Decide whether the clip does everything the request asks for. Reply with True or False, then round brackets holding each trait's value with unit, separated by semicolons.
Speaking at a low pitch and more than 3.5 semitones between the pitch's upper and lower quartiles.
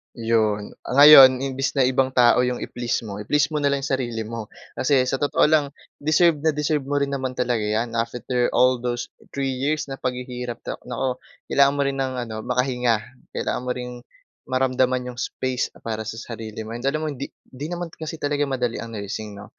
False (130 Hz; 2.8 semitones)